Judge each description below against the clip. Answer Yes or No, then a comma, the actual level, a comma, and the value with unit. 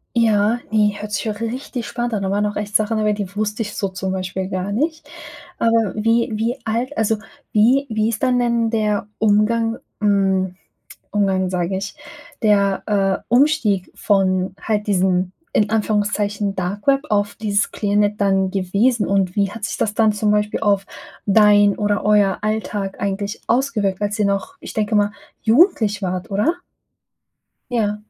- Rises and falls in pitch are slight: Yes, narrow, 2.0 semitones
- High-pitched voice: Yes, high, 210 Hz